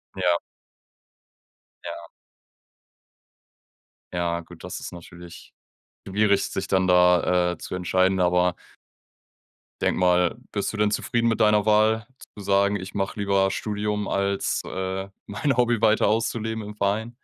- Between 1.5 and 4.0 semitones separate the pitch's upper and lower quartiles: Yes, average, 2.7 semitones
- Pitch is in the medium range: No, low, 100 Hz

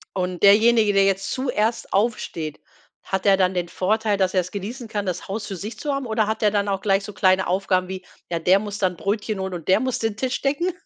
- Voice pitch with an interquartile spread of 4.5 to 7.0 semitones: No, average, 2.7 semitones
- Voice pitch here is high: Yes, high, 200 Hz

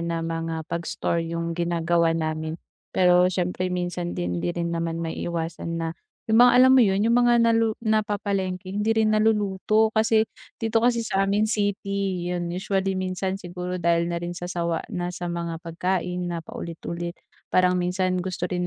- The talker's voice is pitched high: No, medium, 180 Hz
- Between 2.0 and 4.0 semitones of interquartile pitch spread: Yes, average, 3.0 semitones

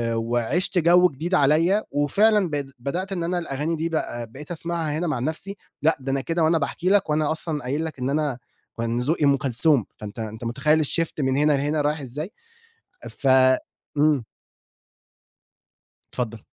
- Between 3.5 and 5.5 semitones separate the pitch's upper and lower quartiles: Yes, average, 3.8 semitones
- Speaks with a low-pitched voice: No, medium, 150 Hz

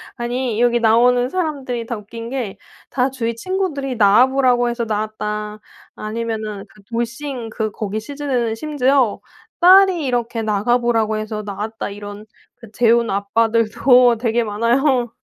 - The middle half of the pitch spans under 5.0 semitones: Yes, average, 2.7 semitones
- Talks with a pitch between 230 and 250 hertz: Yes, high, 235 Hz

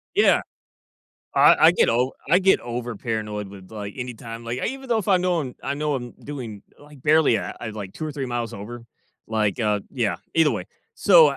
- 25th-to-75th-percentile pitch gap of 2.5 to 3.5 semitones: No, average, 5.3 semitones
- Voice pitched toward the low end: Yes, low, 120 Hz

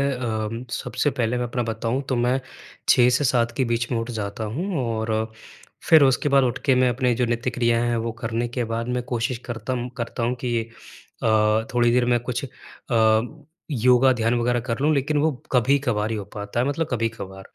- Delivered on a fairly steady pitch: Yes, narrow, 1.9 semitones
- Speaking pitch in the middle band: No, low, 120 Hz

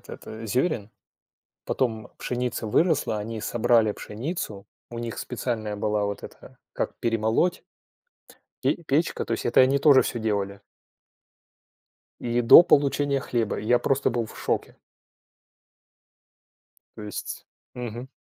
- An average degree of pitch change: Yes, average, 3.4 semitones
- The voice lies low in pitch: Yes, low, 120 Hz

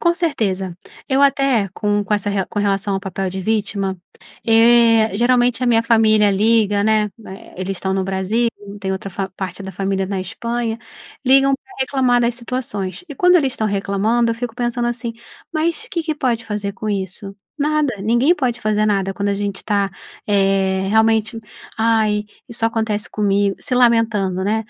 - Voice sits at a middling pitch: No, high, 215 Hz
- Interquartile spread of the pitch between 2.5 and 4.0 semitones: Yes, average, 3.4 semitones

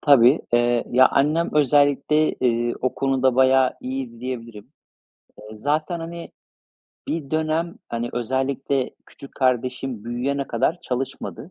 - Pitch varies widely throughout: No, average, 3.2 semitones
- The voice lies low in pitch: Yes, low, 130 Hz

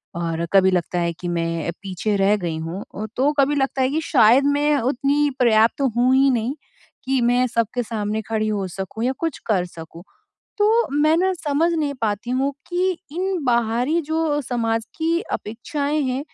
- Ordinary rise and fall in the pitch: No, wide, 6.0 semitones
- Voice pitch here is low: No, high, 245 Hz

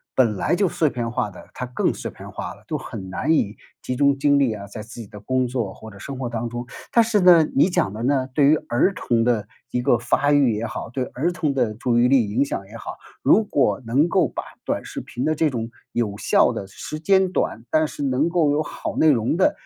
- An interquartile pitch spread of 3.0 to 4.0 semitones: No, average, 4.7 semitones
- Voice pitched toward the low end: Yes, low, 125 Hz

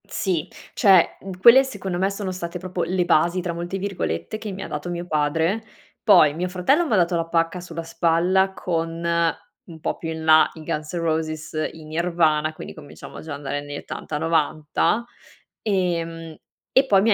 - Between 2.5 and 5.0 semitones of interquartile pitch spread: Yes, average, 2.9 semitones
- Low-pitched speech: No, medium, 170 Hz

